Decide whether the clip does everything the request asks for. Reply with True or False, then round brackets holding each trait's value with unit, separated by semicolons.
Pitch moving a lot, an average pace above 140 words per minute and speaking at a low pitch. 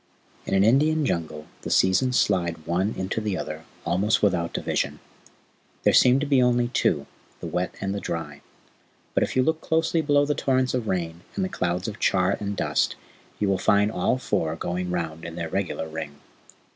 True (6.8 semitones; 190 wpm; 95 Hz)